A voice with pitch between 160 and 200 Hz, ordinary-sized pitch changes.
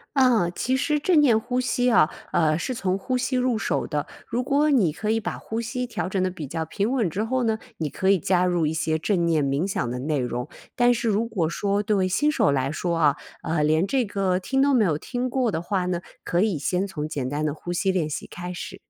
No: high, 190 Hz; wide, 7.1 semitones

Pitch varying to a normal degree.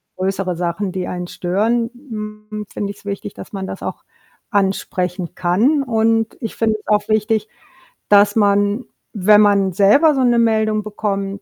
No: narrow, 2.1 semitones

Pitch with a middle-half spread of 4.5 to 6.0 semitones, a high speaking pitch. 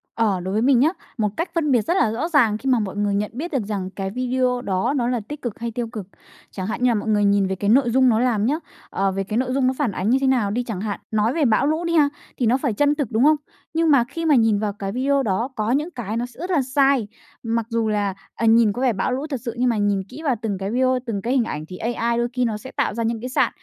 No: average, 3.8 semitones; high, 235 Hz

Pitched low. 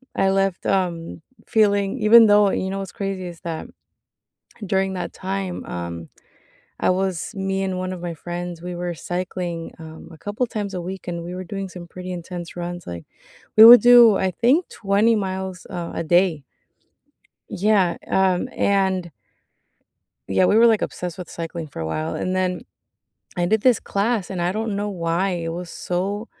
No: medium, 185 Hz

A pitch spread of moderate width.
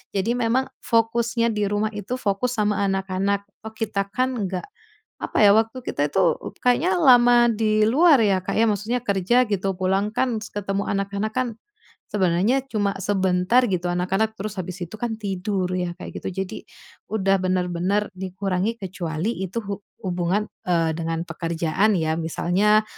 Yes: average, 3.3 semitones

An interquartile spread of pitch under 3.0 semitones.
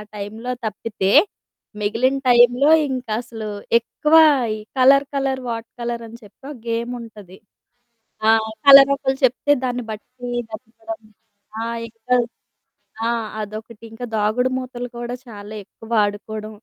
Yes: narrow, 2.6 semitones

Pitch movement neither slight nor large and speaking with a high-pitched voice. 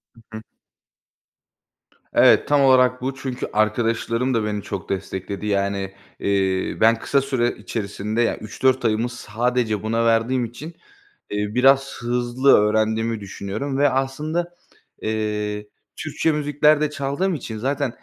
No: average, 4.0 semitones; low, 115 Hz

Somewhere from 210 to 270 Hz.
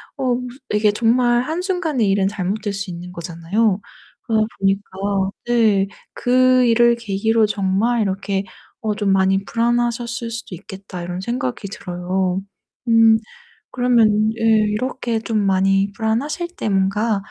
Yes: high, 215 Hz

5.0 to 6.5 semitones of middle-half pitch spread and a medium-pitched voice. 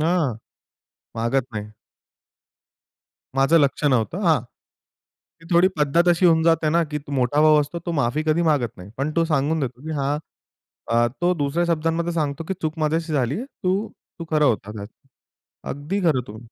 No: average, 3.6 semitones; medium, 150 Hz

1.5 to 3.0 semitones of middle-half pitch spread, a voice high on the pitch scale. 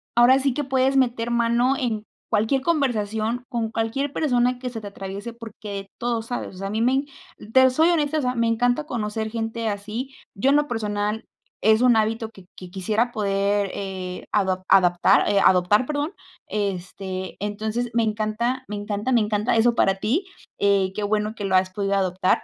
No: average, 3.4 semitones; high, 220 Hz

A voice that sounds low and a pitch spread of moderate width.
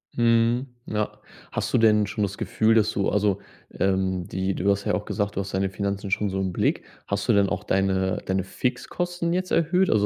Yes: low, 100 Hz; average, 3.0 semitones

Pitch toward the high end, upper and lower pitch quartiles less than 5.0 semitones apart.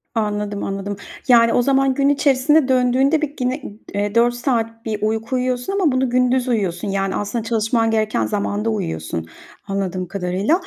Yes: high, 230 Hz; average, 4.0 semitones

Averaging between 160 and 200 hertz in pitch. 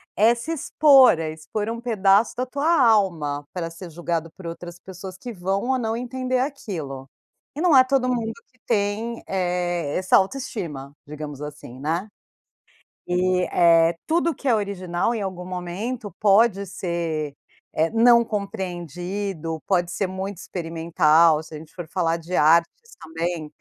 Yes: medium, 185 Hz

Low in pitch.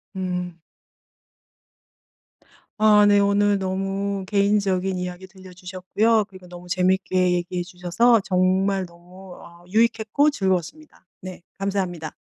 No: high, 190 Hz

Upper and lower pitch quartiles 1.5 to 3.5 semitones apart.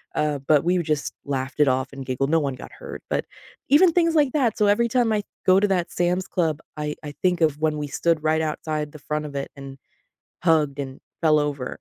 No: average, 4.2 semitones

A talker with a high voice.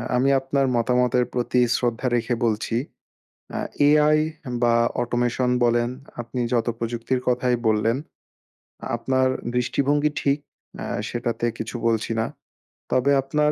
No: low, 125 Hz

